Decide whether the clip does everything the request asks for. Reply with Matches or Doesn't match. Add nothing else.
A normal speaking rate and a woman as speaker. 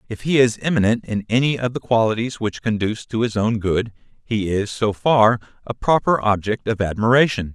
Doesn't match